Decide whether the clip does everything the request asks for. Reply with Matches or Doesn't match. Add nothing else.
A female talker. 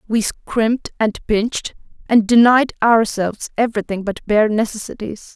Matches